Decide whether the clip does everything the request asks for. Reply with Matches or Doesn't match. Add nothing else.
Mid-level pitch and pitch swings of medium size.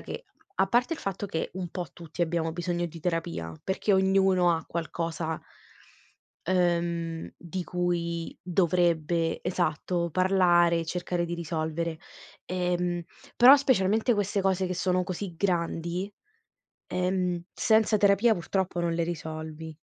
Doesn't match